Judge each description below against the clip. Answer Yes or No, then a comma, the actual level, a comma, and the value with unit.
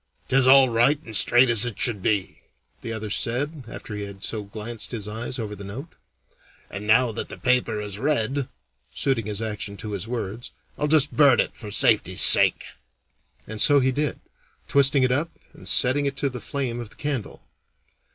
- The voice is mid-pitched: No, low, 120 Hz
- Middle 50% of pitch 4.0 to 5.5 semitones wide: Yes, average, 4.3 semitones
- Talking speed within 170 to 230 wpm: Yes, average, 190 wpm